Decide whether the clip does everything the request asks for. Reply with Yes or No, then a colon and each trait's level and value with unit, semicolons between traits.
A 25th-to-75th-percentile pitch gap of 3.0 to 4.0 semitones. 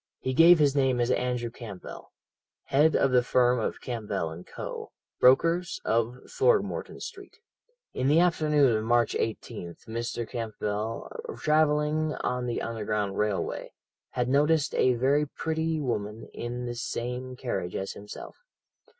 No: average, 4.6 semitones